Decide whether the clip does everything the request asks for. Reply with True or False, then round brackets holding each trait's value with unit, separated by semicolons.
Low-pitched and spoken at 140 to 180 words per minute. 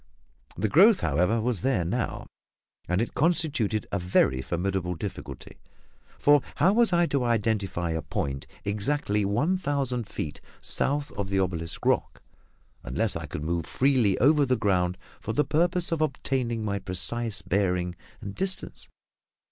True (110 Hz; 150 wpm)